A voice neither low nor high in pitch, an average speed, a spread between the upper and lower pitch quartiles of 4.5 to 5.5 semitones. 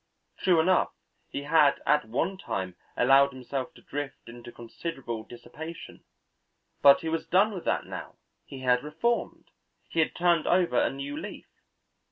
Yes: medium, 145 Hz; average, 155 wpm; average, 5.0 semitones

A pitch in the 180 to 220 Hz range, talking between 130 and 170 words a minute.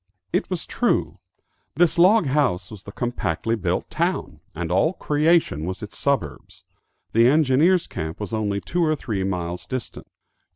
No: low, 115 Hz; average, 155 wpm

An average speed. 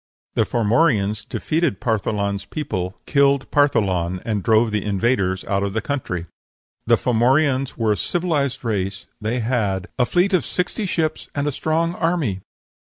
Yes: average, 150 wpm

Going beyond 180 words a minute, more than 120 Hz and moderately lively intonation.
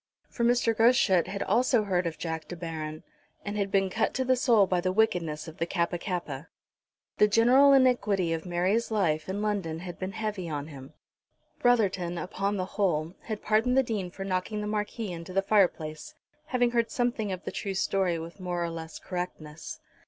Yes: average, 190 wpm; high, 190 Hz; average, 4.2 semitones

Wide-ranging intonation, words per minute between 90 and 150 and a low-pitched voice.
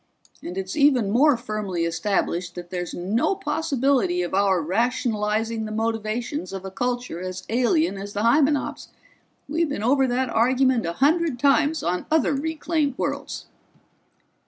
No: wide, 6.5 semitones; average, 145 wpm; high, 230 Hz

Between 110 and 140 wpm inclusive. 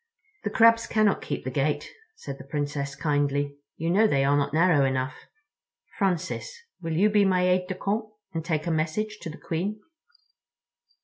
No: average, 175 wpm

